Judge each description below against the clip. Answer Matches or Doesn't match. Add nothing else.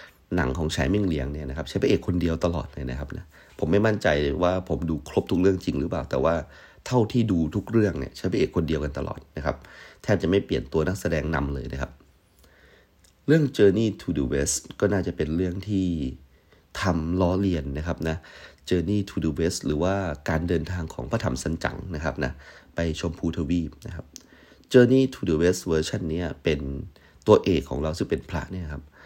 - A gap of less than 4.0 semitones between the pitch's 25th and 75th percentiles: Matches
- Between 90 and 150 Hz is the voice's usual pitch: Doesn't match